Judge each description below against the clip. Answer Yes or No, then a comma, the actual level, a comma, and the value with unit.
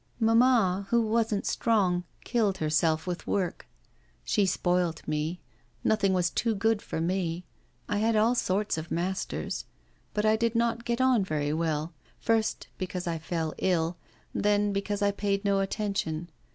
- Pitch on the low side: No, high, 195 Hz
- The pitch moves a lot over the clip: No, average, 4.1 semitones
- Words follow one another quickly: No, average, 150 wpm